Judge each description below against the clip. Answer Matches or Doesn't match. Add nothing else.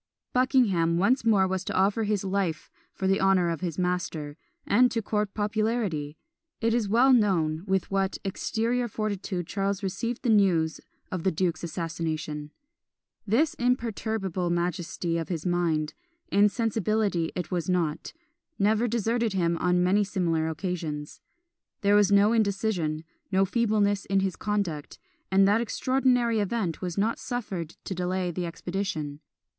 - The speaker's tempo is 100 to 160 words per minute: Matches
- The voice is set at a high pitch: Matches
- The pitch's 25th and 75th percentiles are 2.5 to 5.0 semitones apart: Matches